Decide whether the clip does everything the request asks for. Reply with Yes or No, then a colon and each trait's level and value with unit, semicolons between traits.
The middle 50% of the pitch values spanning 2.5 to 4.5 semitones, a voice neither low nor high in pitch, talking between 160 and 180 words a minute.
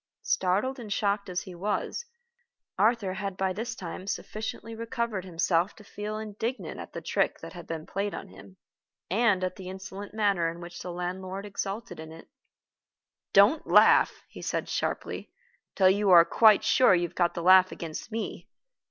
No: average, 3.1 semitones; high, 195 Hz; average, 175 wpm